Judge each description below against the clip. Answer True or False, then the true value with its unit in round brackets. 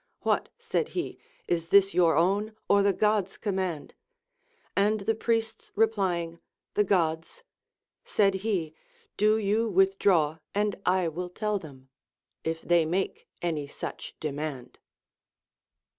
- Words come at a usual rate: False (125 wpm)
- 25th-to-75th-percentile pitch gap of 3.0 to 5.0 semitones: True (4.2 semitones)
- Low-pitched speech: False (190 Hz)